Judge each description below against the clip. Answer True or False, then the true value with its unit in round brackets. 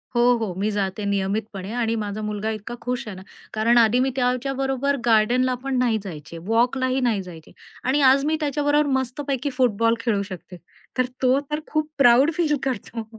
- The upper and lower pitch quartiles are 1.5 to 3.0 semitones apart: False (4.1 semitones)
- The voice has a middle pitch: False (240 Hz)